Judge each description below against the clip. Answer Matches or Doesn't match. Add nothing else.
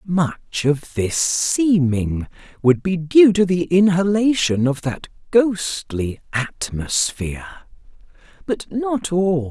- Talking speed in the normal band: Doesn't match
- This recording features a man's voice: Matches